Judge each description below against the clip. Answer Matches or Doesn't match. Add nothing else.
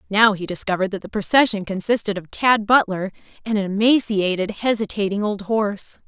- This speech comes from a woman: Matches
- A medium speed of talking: Matches